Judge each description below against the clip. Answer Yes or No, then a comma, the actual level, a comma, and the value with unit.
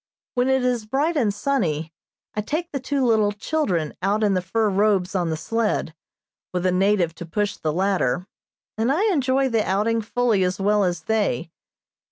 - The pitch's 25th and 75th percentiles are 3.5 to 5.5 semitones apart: Yes, average, 5.1 semitones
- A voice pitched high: Yes, high, 210 Hz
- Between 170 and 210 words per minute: Yes, average, 185 wpm